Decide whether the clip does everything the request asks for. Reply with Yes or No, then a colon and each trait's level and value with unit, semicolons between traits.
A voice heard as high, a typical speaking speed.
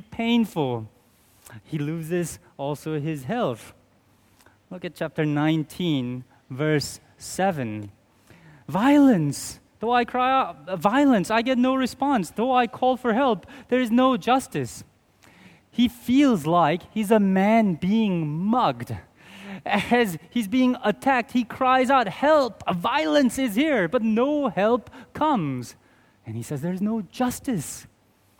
No: high, 200 Hz; slow, 130 wpm